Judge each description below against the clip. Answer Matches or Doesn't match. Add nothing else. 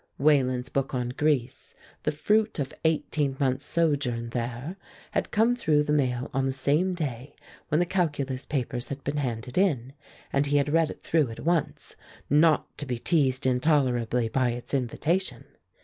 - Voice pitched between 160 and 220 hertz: Doesn't match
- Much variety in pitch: Doesn't match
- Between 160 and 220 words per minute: Matches